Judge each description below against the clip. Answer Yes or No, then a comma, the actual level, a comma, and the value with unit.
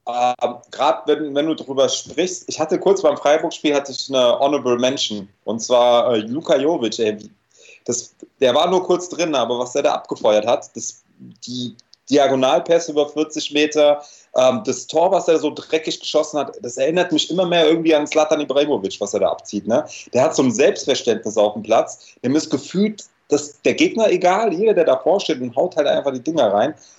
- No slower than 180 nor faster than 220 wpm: Yes, fast, 190 wpm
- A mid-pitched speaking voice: Yes, medium, 150 Hz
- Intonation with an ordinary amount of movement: Yes, average, 3.9 semitones